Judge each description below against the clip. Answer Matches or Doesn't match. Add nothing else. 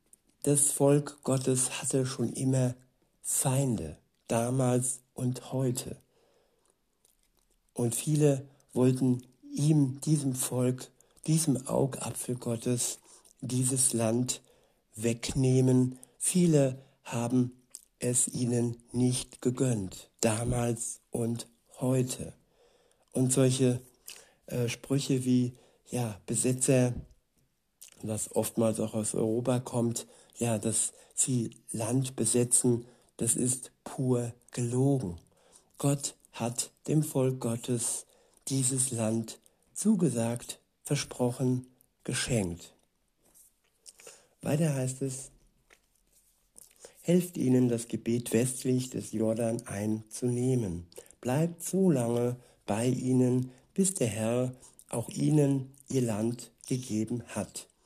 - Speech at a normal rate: Doesn't match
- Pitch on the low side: Matches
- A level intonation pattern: Matches